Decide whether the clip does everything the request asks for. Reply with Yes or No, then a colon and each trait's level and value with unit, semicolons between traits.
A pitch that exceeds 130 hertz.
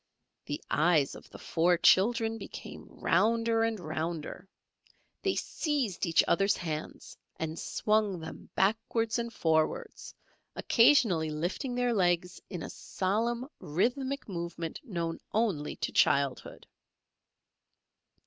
Yes: high, 190 Hz